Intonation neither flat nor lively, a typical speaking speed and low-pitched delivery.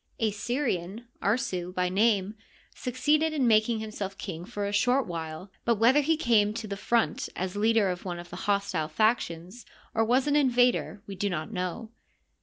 No: average, 4.4 semitones; average, 185 wpm; high, 215 Hz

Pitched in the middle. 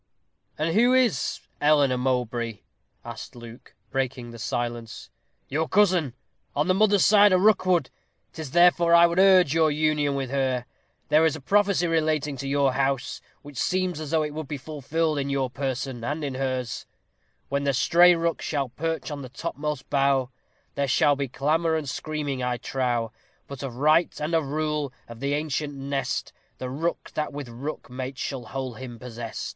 Yes: medium, 145 Hz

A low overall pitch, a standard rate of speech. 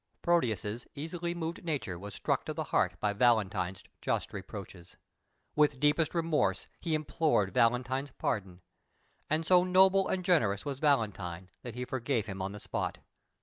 Yes: low, 125 Hz; average, 150 wpm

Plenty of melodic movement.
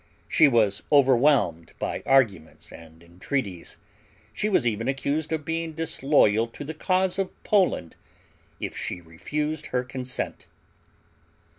Yes: wide, 7.5 semitones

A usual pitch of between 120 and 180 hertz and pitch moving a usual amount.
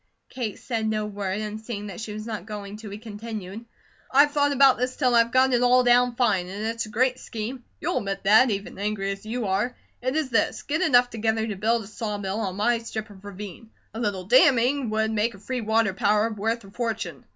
No: high, 220 Hz; average, 3.0 semitones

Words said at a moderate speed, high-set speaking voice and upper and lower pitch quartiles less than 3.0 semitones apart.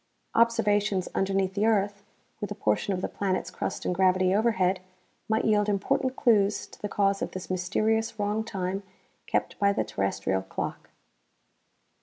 Yes: average, 155 wpm; high, 200 Hz; narrow, 2.4 semitones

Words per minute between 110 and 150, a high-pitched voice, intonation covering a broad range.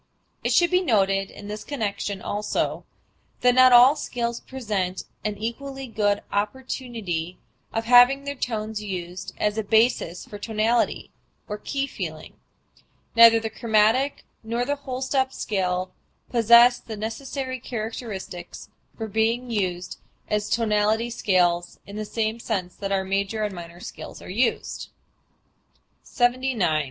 No: average, 140 wpm; high, 220 Hz; average, 3.5 semitones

